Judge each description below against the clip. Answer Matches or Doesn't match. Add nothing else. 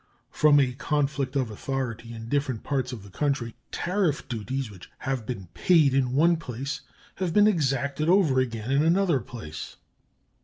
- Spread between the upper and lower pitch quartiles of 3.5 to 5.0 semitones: Matches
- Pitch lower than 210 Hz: Matches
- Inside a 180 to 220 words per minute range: Doesn't match